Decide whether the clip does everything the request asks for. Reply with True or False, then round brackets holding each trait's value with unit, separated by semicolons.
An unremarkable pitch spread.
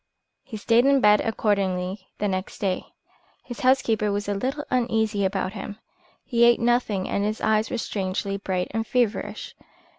True (3.1 semitones)